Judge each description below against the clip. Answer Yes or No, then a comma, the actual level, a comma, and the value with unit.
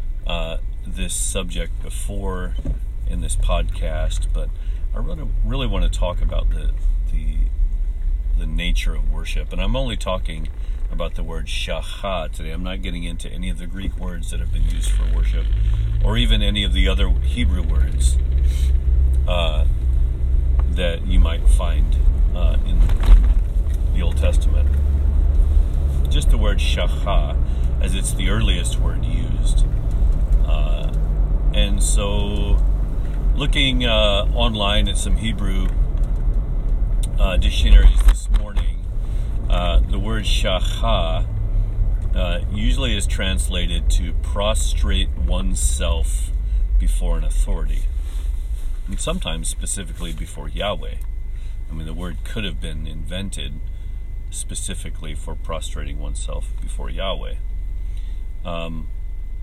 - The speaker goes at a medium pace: No, slow, 120 wpm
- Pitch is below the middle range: Yes, very low, 85 Hz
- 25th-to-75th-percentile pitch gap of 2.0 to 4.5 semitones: No, average, 5.1 semitones